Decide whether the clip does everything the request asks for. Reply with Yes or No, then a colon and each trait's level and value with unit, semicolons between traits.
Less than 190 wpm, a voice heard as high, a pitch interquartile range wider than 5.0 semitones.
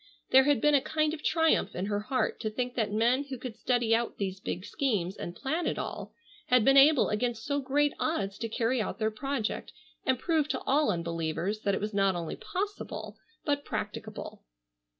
No: average, 200 wpm; high, 245 Hz; wide, 5.4 semitones